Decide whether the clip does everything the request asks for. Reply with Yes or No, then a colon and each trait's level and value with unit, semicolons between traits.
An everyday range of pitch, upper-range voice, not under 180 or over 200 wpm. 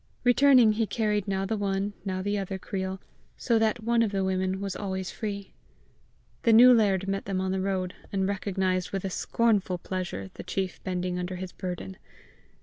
No: narrow, 2.0 semitones; high, 195 Hz; average, 185 wpm